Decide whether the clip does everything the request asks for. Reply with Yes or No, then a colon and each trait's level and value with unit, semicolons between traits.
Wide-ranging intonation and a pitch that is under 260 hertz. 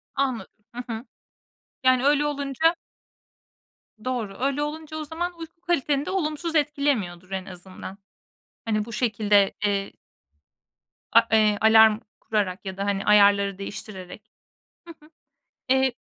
Yes: wide, 6.4 semitones; high, 230 Hz